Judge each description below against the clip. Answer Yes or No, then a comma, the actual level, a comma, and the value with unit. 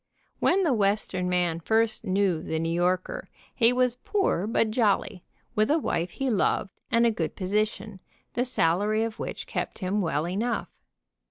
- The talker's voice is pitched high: Yes, high, 210 Hz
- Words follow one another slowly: No, average, 165 wpm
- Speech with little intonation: No, average, 4.0 semitones